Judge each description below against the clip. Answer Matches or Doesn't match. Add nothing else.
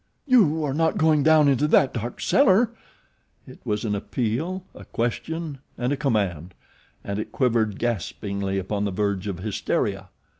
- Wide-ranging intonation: Matches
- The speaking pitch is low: Matches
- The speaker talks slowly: Doesn't match